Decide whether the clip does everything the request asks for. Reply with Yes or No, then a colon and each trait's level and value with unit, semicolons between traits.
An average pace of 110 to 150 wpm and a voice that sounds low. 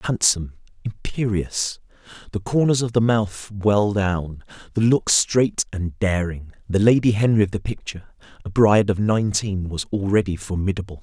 Yes: average, 140 wpm; low, 100 Hz